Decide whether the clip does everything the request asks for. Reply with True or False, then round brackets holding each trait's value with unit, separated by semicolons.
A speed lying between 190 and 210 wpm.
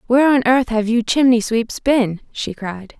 True (200 wpm)